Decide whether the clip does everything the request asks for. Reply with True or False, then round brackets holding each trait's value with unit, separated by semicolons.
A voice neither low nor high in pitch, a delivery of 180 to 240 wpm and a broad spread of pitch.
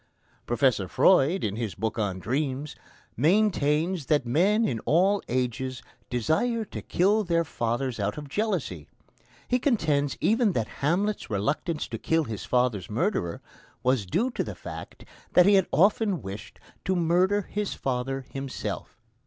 False (145 Hz; 145 wpm; 7.9 semitones)